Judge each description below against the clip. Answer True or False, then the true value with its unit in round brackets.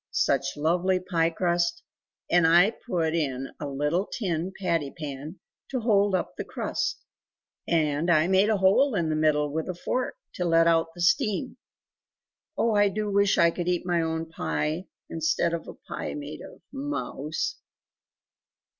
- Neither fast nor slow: True (165 wpm)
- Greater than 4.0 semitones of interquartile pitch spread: False (3.2 semitones)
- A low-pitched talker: False (170 Hz)